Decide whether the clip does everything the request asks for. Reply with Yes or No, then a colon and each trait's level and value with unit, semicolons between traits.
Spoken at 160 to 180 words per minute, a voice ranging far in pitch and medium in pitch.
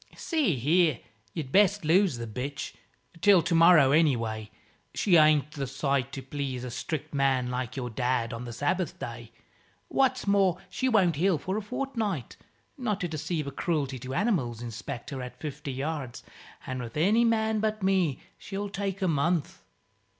Yes: average, 165 wpm; wide, 6.9 semitones; medium, 155 Hz